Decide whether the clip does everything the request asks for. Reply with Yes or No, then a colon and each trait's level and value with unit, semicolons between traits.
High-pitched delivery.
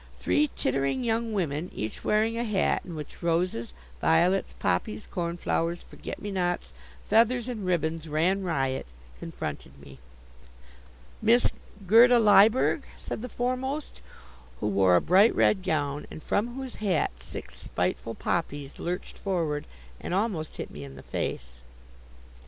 No: medium, 180 Hz